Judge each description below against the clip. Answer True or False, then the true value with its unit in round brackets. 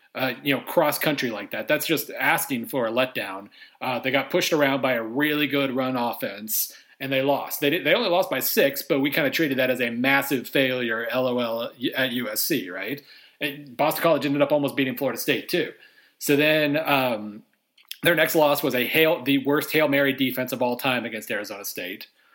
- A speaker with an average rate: False (210 wpm)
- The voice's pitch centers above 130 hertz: True (140 Hz)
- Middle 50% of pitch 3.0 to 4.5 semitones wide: False (2.6 semitones)